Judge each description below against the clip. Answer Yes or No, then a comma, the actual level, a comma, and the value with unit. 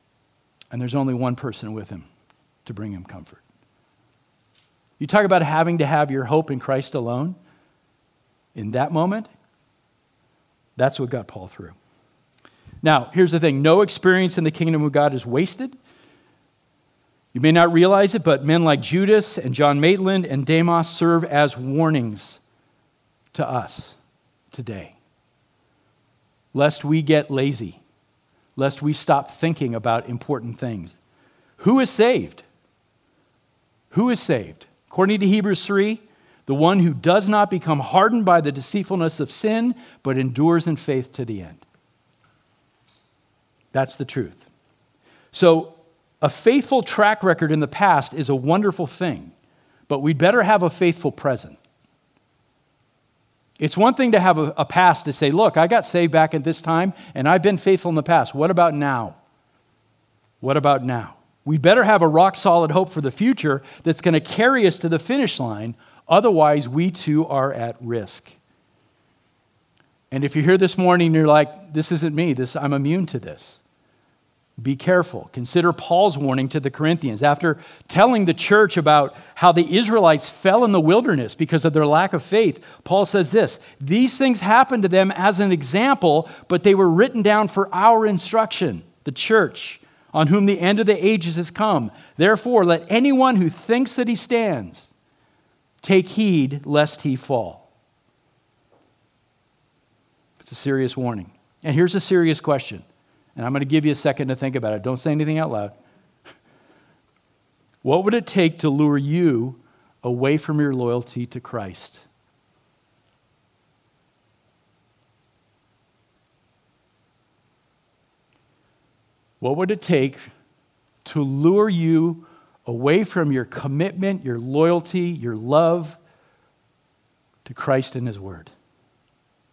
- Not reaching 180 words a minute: Yes, average, 150 wpm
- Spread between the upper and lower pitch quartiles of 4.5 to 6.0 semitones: Yes, wide, 5.4 semitones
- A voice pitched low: No, medium, 155 Hz